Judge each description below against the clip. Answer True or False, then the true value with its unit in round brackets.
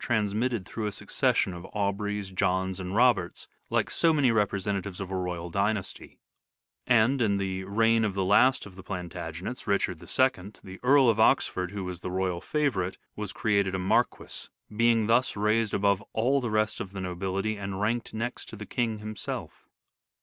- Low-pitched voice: True (100 Hz)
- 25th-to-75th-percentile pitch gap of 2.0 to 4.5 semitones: True (3.2 semitones)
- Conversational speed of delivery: True (180 wpm)